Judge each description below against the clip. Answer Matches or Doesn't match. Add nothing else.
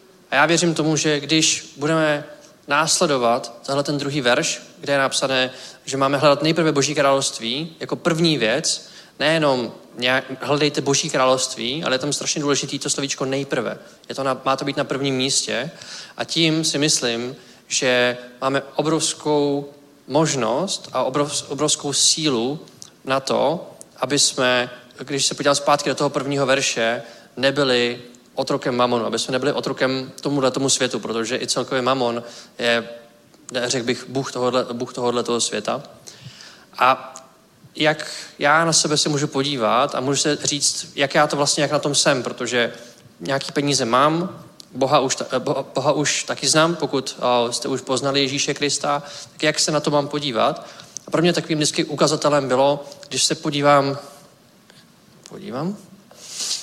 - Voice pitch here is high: Doesn't match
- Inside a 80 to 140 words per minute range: Doesn't match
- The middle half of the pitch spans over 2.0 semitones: Matches